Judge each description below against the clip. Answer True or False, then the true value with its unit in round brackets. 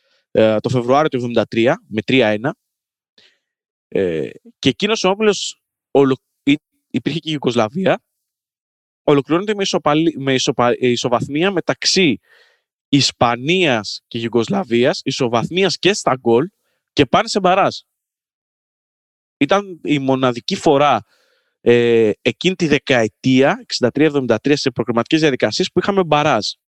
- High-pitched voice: False (140 Hz)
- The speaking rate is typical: False (110 wpm)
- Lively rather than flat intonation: True (7.1 semitones)